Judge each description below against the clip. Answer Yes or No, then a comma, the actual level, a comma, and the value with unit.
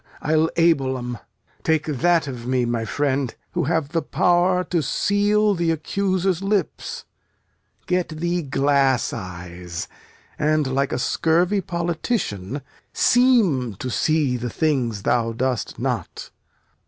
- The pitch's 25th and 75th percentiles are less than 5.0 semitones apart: No, wide, 5.6 semitones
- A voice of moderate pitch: Yes, medium, 150 Hz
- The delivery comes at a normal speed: No, slow, 125 wpm